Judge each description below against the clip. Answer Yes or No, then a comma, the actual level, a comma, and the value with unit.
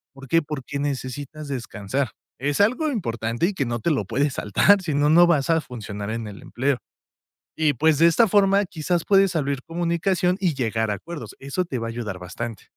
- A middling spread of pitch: No, wide, 6.3 semitones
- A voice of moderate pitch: Yes, medium, 145 Hz